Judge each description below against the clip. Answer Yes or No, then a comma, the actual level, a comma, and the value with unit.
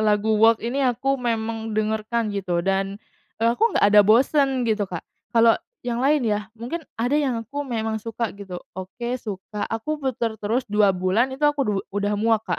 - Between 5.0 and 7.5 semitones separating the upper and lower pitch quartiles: No, average, 3.0 semitones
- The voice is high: Yes, high, 225 Hz